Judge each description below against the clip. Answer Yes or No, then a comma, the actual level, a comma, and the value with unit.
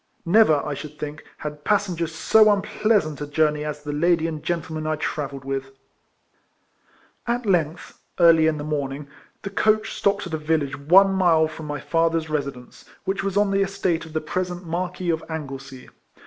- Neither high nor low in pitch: Yes, medium, 160 Hz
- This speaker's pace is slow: No, average, 175 wpm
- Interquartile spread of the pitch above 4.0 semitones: No, average, 3.7 semitones